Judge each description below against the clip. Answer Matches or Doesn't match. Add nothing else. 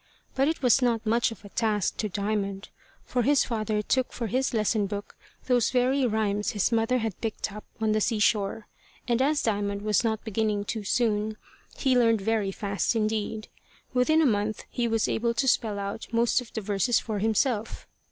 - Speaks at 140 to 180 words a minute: Doesn't match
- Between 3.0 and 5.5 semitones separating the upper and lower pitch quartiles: Doesn't match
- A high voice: Matches